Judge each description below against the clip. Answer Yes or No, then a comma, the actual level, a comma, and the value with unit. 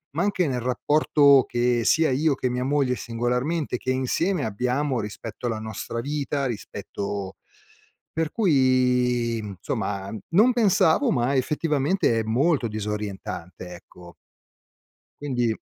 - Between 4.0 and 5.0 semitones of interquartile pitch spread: Yes, average, 4.5 semitones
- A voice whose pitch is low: Yes, low, 125 Hz